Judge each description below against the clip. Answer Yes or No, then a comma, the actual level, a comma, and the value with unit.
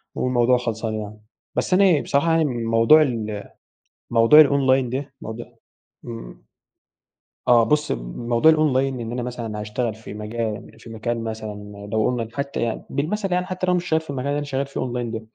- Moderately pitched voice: No, low, 120 Hz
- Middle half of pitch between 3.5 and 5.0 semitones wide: Yes, average, 4.1 semitones